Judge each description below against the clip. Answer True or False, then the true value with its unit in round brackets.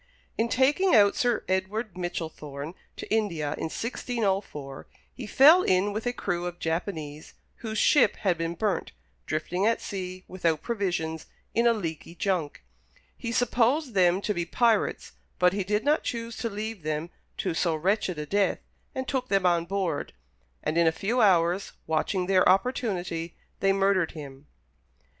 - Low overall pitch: False (190 Hz)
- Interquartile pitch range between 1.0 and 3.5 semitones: False (4.9 semitones)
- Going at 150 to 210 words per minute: True (160 wpm)